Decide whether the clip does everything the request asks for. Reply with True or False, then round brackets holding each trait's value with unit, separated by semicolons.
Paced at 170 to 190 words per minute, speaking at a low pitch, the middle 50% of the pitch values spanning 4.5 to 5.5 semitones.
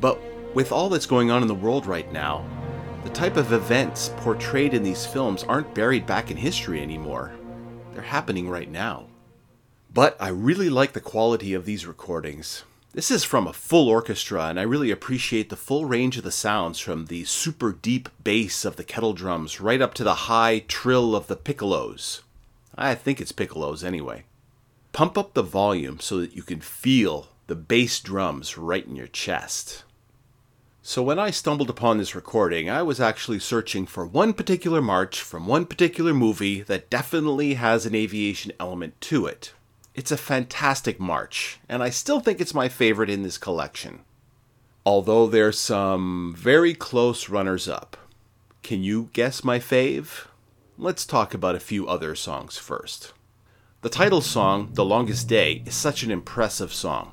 True (175 wpm; 115 Hz; 4.8 semitones)